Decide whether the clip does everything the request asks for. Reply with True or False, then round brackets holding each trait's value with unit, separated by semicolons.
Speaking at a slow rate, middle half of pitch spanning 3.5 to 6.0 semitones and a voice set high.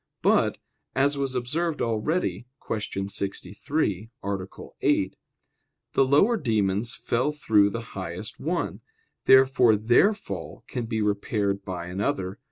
False (120 wpm; 5.2 semitones; 115 Hz)